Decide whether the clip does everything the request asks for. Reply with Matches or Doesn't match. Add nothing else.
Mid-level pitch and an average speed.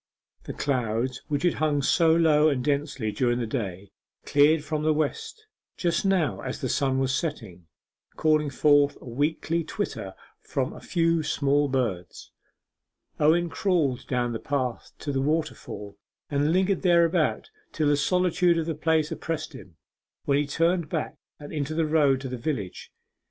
Matches